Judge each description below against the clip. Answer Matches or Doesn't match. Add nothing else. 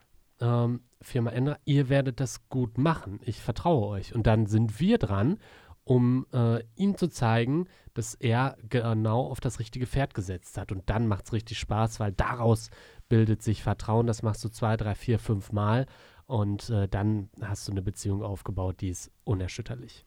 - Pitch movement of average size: Matches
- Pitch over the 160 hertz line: Doesn't match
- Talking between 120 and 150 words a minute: Doesn't match